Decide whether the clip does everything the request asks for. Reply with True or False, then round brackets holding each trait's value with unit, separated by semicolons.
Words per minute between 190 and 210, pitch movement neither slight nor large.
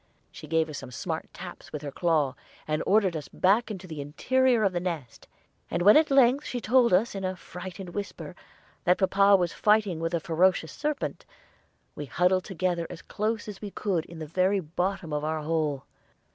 True (195 wpm; 4.0 semitones)